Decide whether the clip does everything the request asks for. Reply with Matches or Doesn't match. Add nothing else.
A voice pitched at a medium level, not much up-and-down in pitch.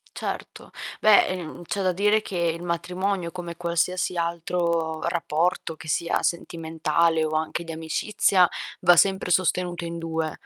Matches